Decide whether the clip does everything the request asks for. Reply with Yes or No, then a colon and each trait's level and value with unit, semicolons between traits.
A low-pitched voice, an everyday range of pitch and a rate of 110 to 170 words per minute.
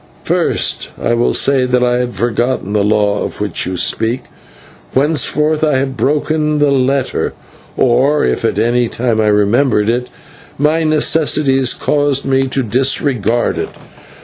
Yes: low, 130 Hz; average, 3.5 semitones; average, 150 wpm